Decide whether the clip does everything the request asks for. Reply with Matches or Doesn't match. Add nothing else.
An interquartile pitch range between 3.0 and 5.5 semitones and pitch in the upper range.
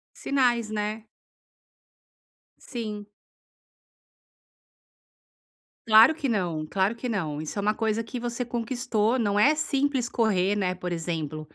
Matches